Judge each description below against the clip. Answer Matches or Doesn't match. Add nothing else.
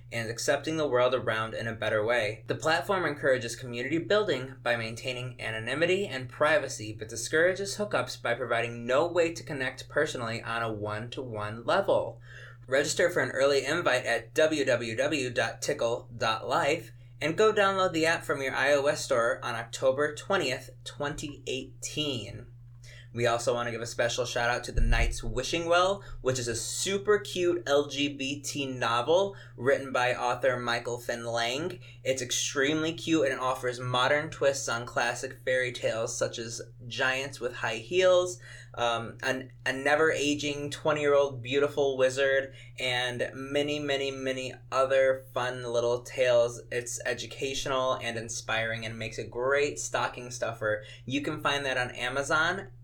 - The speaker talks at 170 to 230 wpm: Doesn't match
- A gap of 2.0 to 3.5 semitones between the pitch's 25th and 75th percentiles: Matches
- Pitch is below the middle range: Matches